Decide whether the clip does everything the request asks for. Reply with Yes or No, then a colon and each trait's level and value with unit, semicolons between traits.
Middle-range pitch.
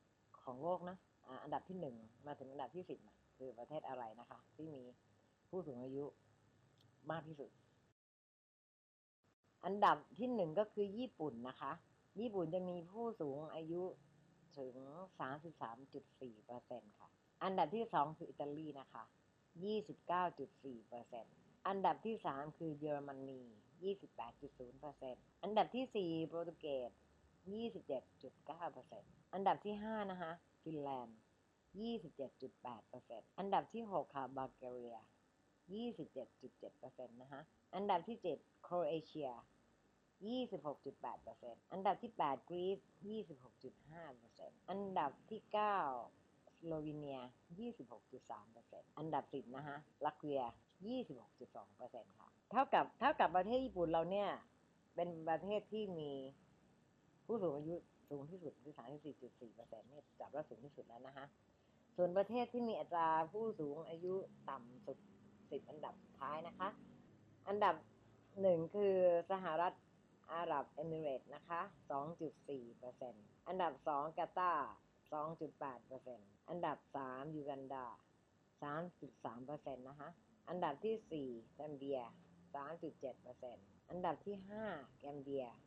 Yes: medium, 150 Hz